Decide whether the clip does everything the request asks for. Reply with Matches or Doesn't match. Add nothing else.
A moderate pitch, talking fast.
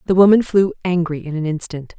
Matches